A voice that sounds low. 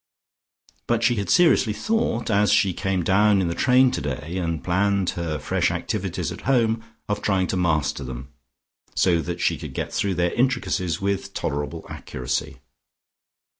Yes: very low, 95 Hz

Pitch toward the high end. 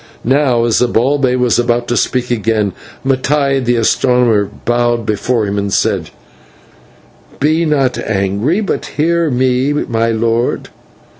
No: low, 120 Hz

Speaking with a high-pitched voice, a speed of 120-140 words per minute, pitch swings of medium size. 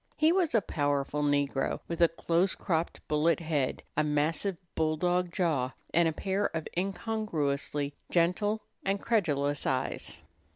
No: medium, 165 Hz; slow, 135 wpm; average, 4.7 semitones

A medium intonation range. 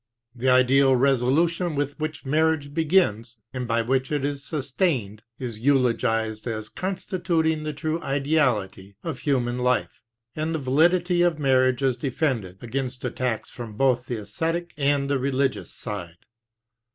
Yes: average, 4.2 semitones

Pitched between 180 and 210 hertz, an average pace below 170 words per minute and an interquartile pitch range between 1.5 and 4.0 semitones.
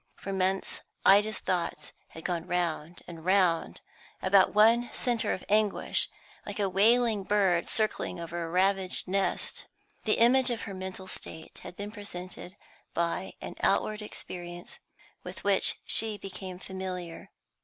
Yes: high, 190 Hz; average, 140 wpm; average, 2.9 semitones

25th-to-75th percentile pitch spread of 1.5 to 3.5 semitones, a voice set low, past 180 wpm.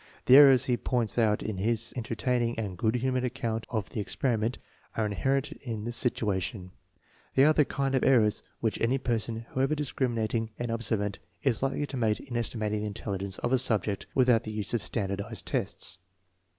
Yes: average, 3.1 semitones; low, 115 Hz; average, 190 wpm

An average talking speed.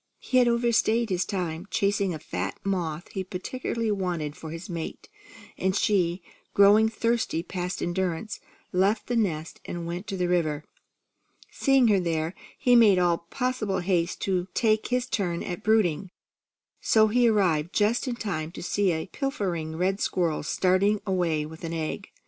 Yes: average, 160 wpm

